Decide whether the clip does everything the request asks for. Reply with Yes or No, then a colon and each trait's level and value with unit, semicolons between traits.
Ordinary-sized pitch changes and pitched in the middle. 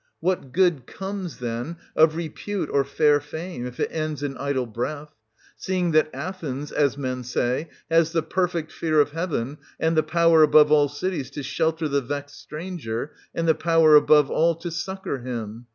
Yes: average, 3.1 semitones; medium, 155 Hz